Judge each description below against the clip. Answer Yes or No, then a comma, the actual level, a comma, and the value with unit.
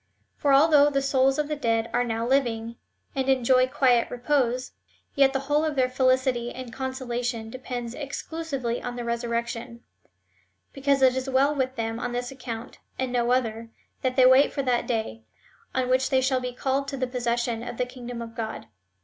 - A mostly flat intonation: Yes, narrow, 2.1 semitones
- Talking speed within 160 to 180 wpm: No, average, 190 wpm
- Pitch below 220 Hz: No, very high, 255 Hz